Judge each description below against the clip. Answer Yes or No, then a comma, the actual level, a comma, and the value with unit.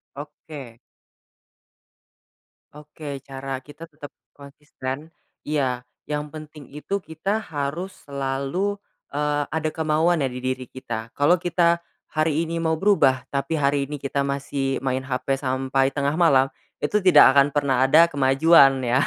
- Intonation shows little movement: No, average, 3.0 semitones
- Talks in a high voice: No, medium, 145 Hz